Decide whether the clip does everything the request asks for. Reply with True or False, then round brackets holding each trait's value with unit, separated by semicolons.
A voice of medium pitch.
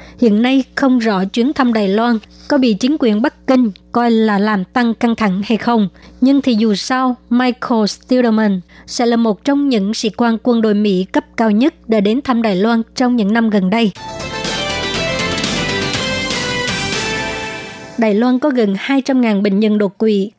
False (230 Hz)